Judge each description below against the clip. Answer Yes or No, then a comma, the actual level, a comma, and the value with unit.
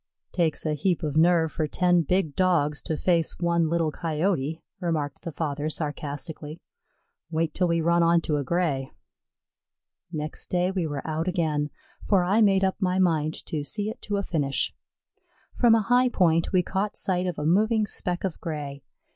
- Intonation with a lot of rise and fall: No, average, 3.2 semitones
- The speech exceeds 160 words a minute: Yes, average, 175 wpm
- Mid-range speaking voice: Yes, medium, 170 Hz